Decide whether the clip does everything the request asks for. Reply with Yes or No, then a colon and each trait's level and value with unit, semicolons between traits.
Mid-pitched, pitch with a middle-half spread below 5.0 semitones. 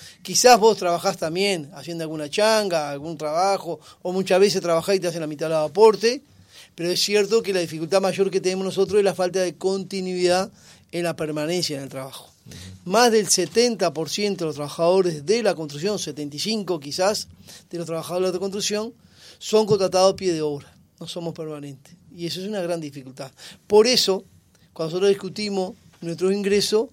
Yes: medium, 180 Hz; average, 3.5 semitones